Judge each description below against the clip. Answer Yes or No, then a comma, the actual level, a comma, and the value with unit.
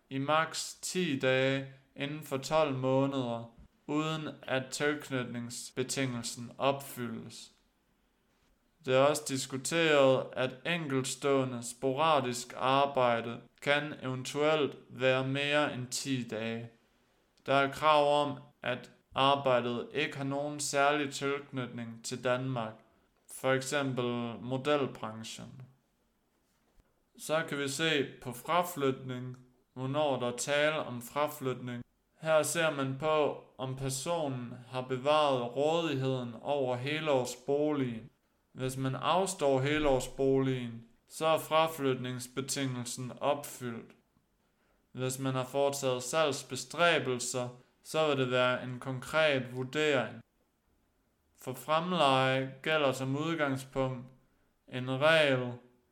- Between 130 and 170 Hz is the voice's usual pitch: Yes, low, 135 Hz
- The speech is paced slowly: Yes, slow, 100 wpm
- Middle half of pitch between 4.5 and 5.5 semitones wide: No, narrow, 2.5 semitones